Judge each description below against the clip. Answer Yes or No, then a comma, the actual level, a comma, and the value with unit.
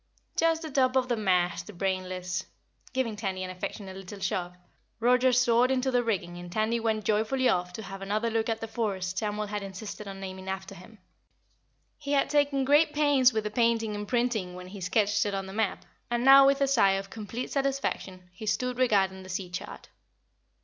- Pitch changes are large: No, average, 4.7 semitones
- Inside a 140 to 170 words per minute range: No, average, 200 wpm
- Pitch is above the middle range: Yes, high, 215 Hz